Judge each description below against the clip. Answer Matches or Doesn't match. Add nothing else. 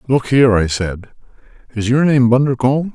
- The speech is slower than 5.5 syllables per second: Doesn't match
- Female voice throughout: Doesn't match